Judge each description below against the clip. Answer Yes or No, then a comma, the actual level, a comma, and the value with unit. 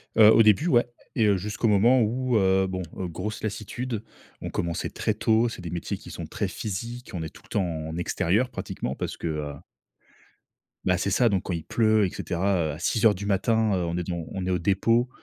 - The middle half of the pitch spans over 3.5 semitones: Yes, average, 3.9 semitones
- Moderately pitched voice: No, low, 100 Hz